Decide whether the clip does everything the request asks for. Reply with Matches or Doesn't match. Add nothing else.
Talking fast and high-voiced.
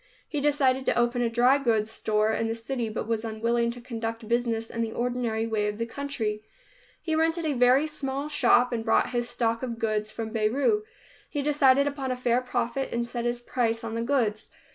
Matches